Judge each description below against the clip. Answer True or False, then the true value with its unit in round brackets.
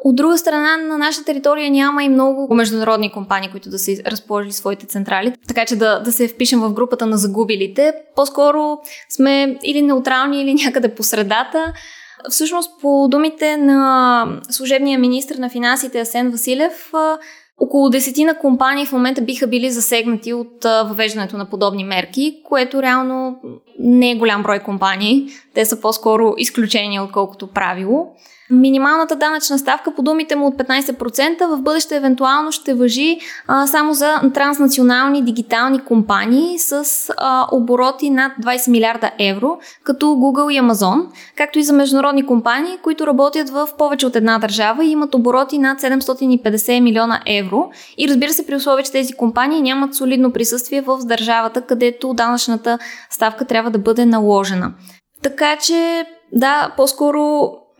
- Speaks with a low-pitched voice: False (260 Hz)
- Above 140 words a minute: True (150 wpm)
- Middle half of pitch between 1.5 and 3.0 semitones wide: False (3.8 semitones)